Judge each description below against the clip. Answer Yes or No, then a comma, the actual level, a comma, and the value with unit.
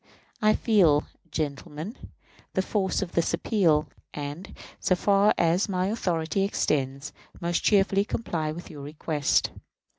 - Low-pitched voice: No, medium, 175 Hz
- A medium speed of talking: No, slow, 125 wpm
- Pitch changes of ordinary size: Yes, average, 4.6 semitones